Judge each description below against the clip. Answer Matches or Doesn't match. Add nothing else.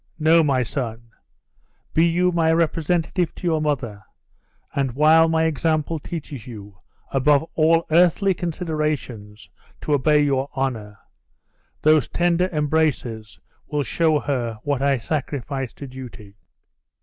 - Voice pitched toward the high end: Doesn't match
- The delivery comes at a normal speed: Doesn't match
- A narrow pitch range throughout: Doesn't match